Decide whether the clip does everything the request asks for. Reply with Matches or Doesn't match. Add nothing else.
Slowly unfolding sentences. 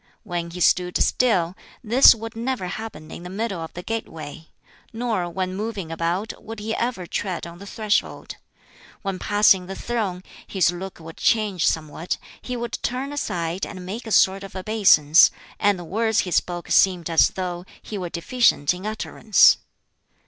Doesn't match